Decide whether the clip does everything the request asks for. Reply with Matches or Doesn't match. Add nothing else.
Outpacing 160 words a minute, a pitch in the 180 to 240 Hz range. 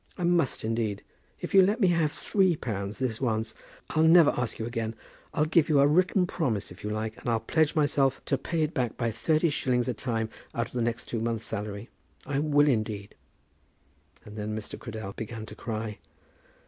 Doesn't match